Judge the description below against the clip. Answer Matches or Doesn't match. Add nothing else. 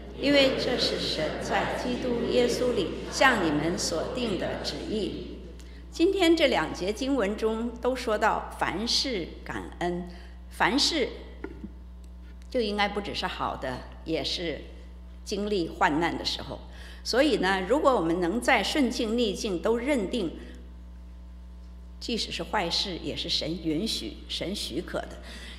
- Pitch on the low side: Doesn't match